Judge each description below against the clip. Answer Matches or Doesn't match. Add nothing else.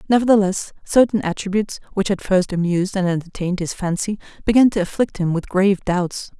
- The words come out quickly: Doesn't match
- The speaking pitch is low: Doesn't match